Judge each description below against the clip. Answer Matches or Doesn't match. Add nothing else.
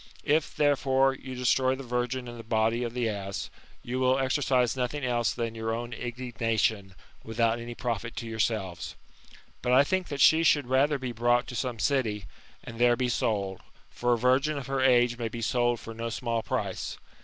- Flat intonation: Matches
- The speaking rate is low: Doesn't match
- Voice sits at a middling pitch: Doesn't match